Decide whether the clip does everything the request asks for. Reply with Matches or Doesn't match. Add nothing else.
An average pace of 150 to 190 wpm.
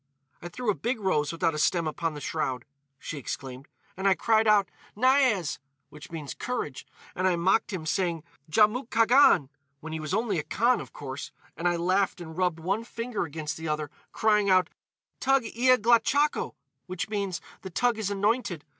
Matches